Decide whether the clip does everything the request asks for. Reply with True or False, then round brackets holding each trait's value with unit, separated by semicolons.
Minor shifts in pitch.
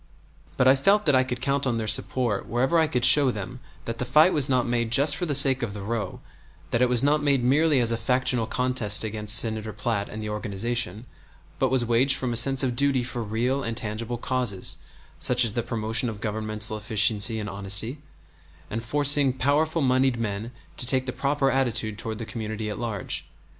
False (3.4 semitones)